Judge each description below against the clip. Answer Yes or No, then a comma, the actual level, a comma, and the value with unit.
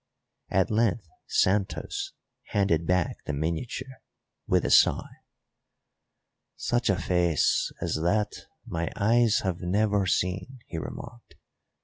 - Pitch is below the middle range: Yes, very low, 95 Hz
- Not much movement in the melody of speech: No, average, 4.3 semitones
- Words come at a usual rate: No, slow, 110 wpm